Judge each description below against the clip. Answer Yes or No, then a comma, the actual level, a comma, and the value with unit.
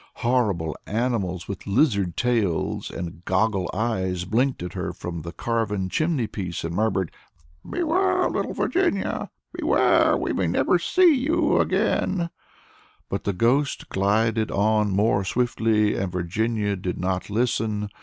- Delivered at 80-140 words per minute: Yes, slow, 135 wpm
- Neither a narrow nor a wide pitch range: Yes, average, 4.5 semitones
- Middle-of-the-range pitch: No, low, 105 Hz